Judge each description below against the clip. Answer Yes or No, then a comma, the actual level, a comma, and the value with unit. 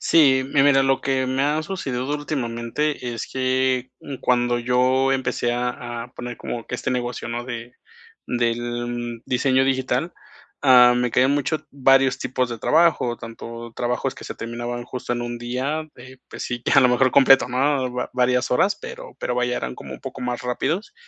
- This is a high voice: No, low, 125 Hz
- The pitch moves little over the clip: Yes, narrow, 1.9 semitones